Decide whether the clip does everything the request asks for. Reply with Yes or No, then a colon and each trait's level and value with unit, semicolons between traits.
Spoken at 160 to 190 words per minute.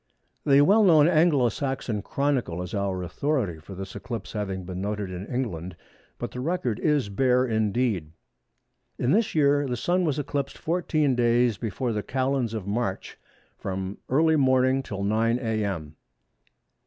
No: average, 150 wpm